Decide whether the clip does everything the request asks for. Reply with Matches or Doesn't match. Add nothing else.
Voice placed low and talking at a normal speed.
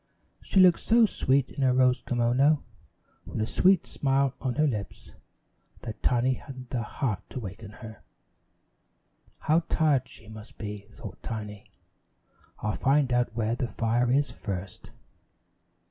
Matches